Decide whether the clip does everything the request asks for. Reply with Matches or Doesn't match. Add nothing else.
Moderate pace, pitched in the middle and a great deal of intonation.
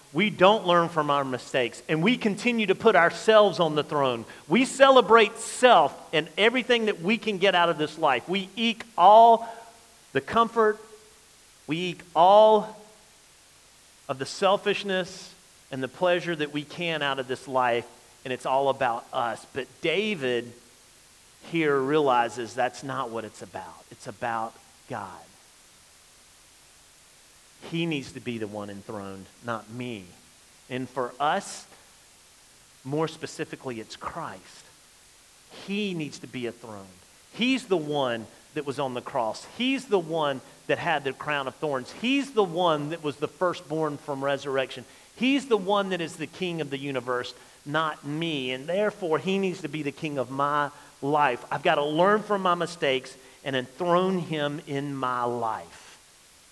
Matches